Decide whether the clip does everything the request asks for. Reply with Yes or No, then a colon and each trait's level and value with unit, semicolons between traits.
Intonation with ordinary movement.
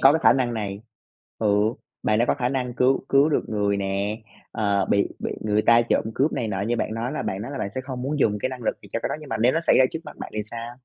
Yes: average, 3.8 semitones